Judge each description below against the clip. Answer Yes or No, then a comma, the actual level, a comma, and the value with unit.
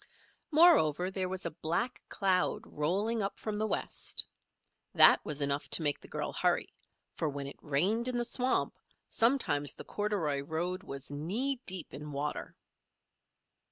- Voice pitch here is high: No, medium, 180 Hz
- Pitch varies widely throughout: Yes, wide, 6.7 semitones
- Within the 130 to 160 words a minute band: Yes, average, 155 wpm